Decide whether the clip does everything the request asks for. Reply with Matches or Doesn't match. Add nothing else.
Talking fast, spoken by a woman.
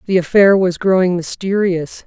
Doesn't match